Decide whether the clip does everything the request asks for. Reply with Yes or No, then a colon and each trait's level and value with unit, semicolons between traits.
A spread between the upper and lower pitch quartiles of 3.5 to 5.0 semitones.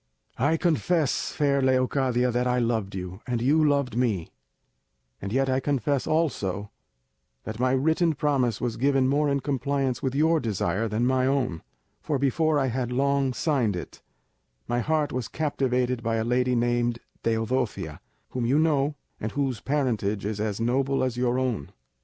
No: average, 3.1 semitones